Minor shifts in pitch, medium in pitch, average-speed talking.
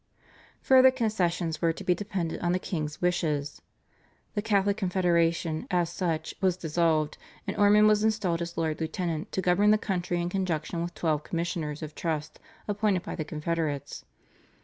No: average, 3.2 semitones; medium, 175 Hz; average, 160 wpm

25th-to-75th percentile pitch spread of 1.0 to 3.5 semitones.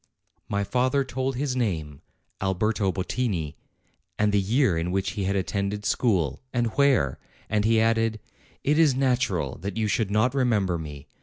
No: average, 4.9 semitones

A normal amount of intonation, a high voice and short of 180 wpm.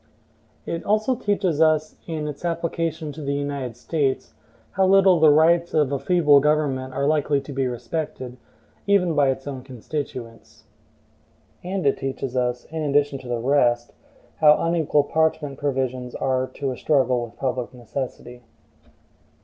No: average, 3.5 semitones; medium, 145 Hz; average, 150 wpm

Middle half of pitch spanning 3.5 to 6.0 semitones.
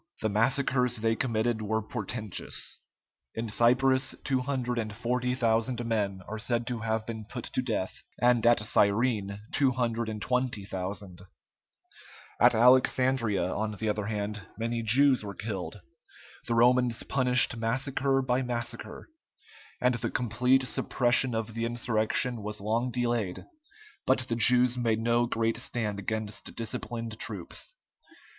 No: narrow, 2.4 semitones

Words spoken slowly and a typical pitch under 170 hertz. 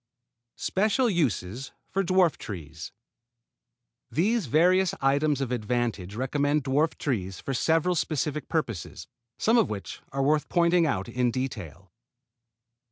Yes: slow, 125 wpm; medium, 140 Hz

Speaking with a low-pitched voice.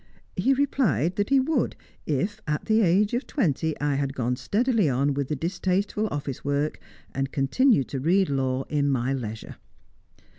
No: medium, 150 Hz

